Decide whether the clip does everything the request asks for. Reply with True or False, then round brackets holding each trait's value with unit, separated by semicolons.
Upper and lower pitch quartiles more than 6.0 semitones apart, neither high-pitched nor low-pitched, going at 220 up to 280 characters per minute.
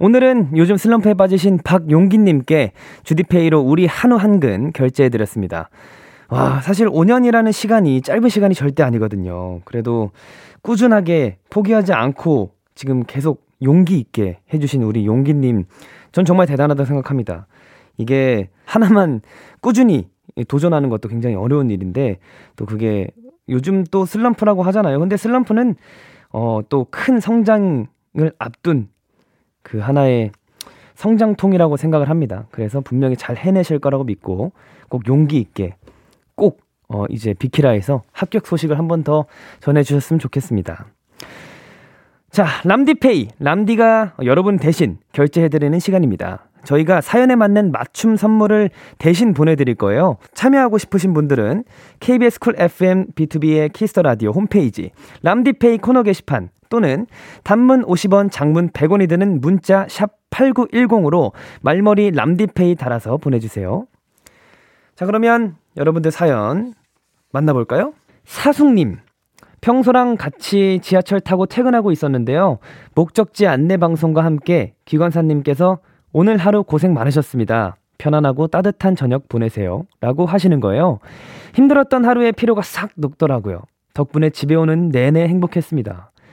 False (7.6 semitones; 160 Hz; 310 characters per minute)